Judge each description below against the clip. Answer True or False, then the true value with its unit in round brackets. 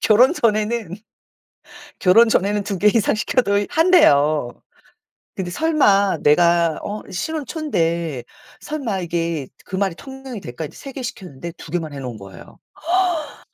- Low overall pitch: False (195 Hz)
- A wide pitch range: True (6.3 semitones)